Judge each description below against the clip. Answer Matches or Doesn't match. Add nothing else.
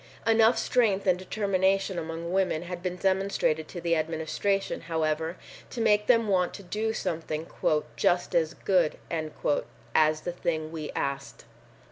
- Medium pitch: Matches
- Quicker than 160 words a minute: Doesn't match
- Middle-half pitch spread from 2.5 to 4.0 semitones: Matches